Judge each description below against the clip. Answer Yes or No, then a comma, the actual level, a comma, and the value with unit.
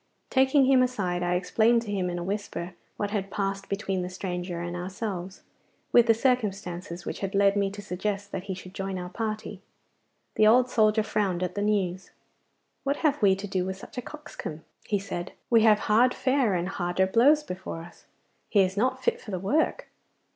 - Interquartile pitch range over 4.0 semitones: No, average, 3.4 semitones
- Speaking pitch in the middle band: No, high, 200 Hz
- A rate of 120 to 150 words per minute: No, average, 200 wpm